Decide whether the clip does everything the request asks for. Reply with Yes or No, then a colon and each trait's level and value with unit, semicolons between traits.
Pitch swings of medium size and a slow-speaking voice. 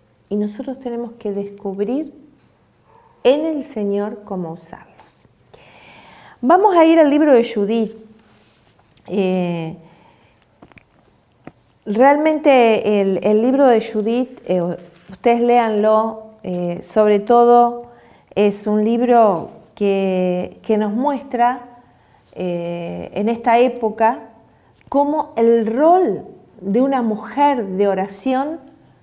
Yes: average, 4.2 semitones; slow, 100 wpm